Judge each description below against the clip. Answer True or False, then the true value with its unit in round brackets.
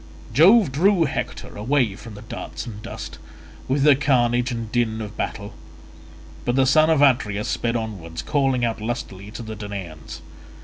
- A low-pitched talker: True (120 Hz)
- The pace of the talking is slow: False (165 wpm)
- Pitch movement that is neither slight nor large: True (4.4 semitones)